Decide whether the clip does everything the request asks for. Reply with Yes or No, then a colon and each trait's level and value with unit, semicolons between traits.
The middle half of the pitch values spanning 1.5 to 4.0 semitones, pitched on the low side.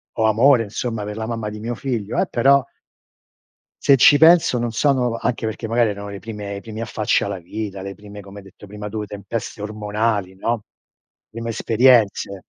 Yes: narrow, 2.4 semitones; low, 110 Hz